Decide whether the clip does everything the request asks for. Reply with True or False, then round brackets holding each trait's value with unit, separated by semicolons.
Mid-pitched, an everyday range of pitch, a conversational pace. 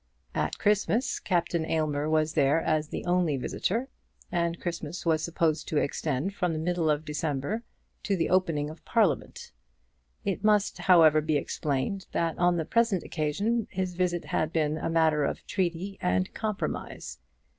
True (165 Hz; 3.3 semitones; 155 wpm)